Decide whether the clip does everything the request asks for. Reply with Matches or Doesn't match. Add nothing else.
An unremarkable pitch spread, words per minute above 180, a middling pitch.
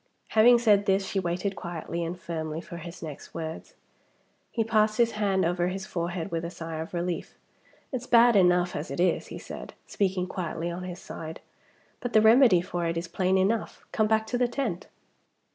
Matches